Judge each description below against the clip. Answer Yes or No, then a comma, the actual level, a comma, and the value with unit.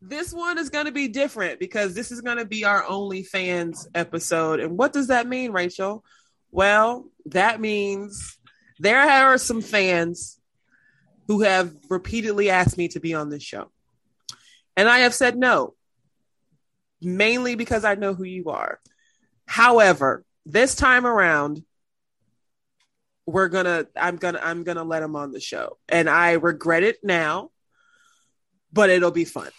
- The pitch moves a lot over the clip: Yes, wide, 6.2 semitones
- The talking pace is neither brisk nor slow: Yes, average, 160 wpm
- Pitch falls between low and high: No, high, 200 Hz